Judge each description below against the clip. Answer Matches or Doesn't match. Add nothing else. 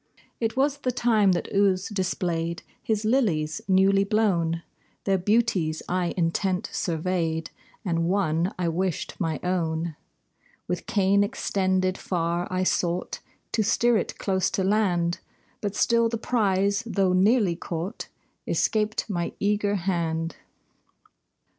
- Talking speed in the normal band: Doesn't match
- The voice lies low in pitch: Doesn't match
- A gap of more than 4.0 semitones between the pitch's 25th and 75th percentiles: Doesn't match